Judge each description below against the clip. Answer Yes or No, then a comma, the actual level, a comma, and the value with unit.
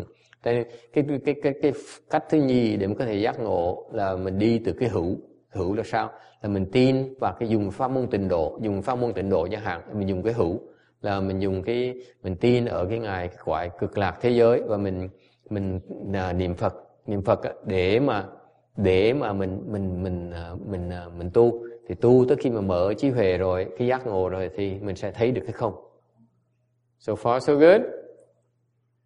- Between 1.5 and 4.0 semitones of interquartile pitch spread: No, average, 4.4 semitones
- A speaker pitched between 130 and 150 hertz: No, low, 110 Hz